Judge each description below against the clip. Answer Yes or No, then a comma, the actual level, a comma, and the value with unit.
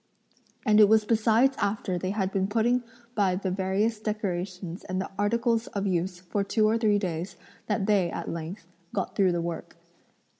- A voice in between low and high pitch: No, high, 200 Hz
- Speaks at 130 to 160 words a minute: No, average, 175 wpm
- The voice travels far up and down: No, average, 2.8 semitones